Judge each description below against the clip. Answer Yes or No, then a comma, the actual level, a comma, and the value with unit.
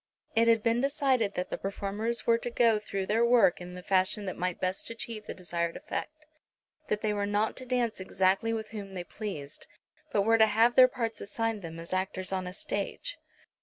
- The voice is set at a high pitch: Yes, high, 210 Hz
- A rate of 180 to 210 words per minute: Yes, fast, 205 wpm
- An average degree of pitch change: Yes, average, 3.5 semitones